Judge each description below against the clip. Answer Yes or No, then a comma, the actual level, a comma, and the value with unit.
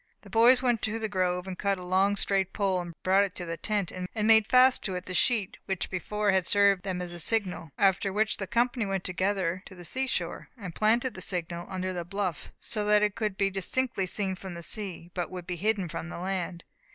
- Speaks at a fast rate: Yes, fast, 230 wpm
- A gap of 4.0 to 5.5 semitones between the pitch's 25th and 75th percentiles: No, average, 2.7 semitones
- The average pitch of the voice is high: Yes, high, 195 Hz